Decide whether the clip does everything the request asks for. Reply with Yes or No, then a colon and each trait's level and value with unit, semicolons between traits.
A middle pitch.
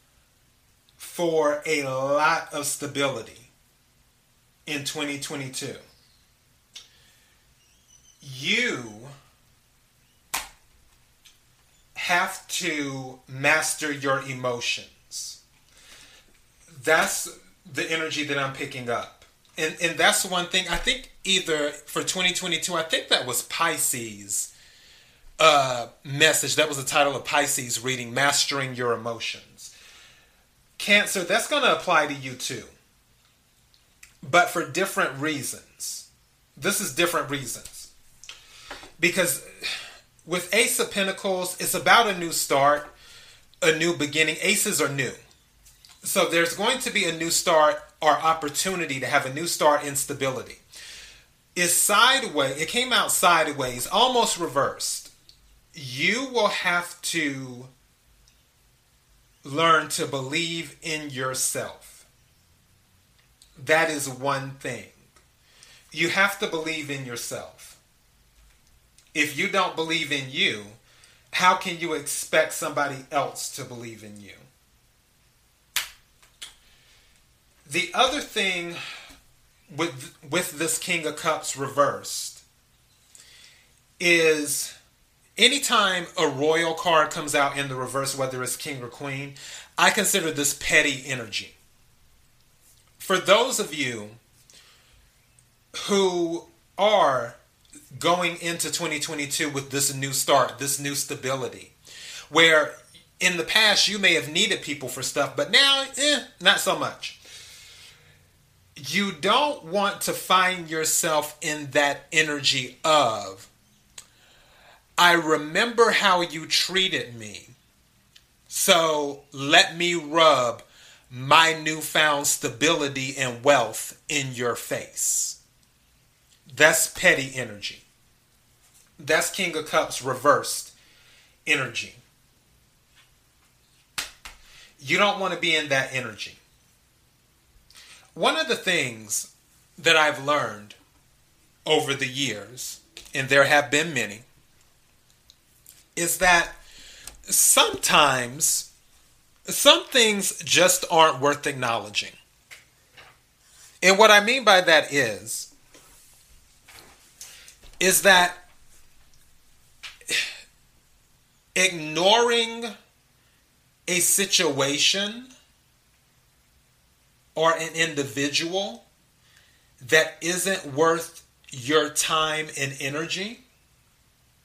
Yes: medium, 150 Hz